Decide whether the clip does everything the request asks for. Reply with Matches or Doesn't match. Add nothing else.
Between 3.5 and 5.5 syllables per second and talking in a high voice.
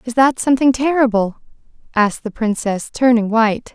Matches